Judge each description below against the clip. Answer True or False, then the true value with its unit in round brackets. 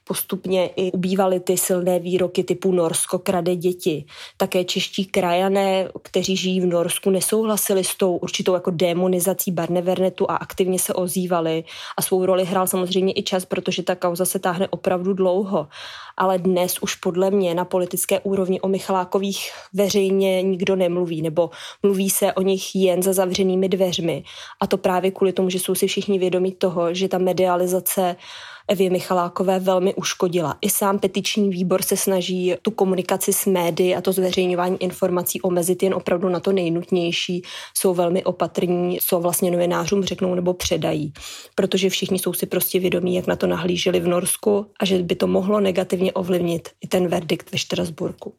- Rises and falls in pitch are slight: True (1.2 semitones)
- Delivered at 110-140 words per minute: False (165 wpm)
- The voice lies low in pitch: False (185 Hz)